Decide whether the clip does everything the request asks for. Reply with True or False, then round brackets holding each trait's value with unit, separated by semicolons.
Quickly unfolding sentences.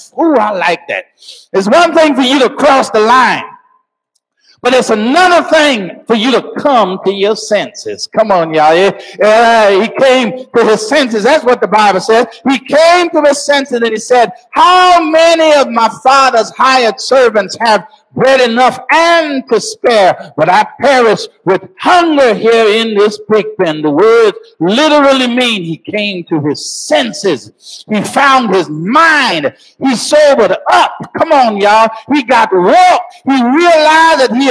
False (165 wpm)